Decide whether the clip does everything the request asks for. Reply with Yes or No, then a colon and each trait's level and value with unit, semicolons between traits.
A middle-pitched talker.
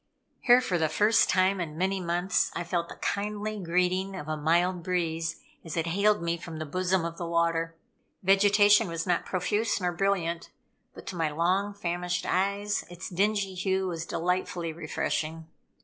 Yes: medium, 180 Hz